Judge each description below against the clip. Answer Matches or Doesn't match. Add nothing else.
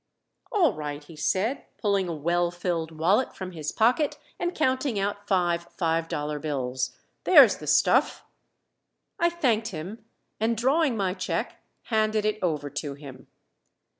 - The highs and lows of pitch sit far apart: Matches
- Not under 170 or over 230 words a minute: Doesn't match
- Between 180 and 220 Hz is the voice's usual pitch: Matches